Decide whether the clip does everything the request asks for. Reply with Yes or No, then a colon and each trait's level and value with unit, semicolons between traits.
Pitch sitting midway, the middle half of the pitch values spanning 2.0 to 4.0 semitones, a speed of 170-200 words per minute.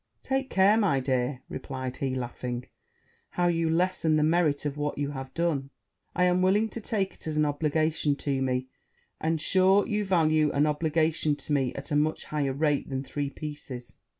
Yes: medium, 150 Hz; average, 3.7 semitones; average, 185 wpm